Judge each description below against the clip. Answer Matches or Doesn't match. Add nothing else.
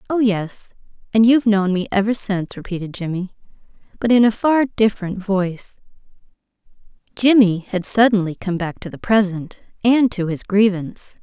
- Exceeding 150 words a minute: Doesn't match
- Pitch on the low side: Doesn't match